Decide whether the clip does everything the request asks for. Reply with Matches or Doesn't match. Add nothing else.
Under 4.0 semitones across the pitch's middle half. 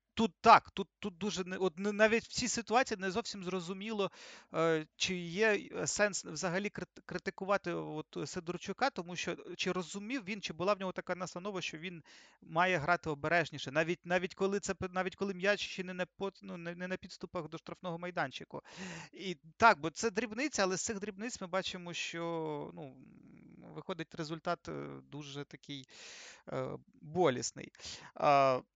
Matches